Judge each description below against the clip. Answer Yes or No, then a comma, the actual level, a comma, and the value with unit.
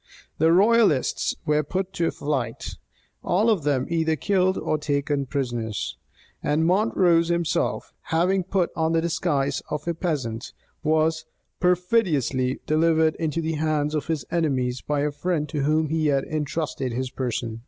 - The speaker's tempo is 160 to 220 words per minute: No, average, 150 wpm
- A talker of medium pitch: Yes, medium, 155 Hz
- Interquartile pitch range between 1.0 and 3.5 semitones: Yes, average, 3.1 semitones